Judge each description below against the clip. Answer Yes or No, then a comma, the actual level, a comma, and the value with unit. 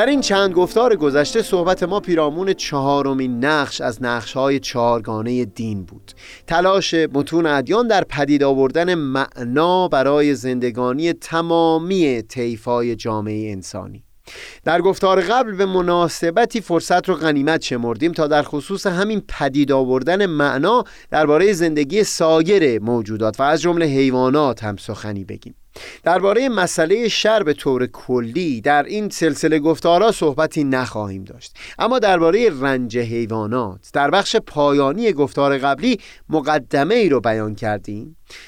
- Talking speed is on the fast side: No, average, 130 wpm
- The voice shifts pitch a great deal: Yes, wide, 6.0 semitones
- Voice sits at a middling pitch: Yes, medium, 145 Hz